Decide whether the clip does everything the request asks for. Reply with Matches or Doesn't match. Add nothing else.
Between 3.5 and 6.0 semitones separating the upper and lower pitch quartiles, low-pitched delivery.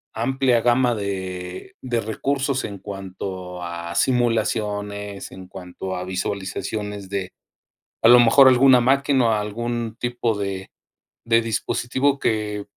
Matches